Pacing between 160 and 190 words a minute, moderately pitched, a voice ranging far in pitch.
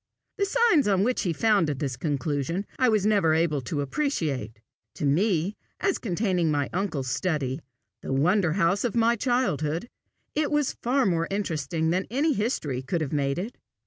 Yes: average, 170 wpm; medium, 175 Hz; wide, 7.3 semitones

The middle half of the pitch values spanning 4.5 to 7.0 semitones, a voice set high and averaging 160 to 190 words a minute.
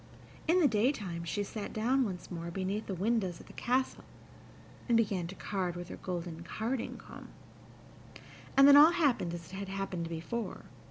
Yes: average, 5.1 semitones; high, 195 Hz; average, 175 wpm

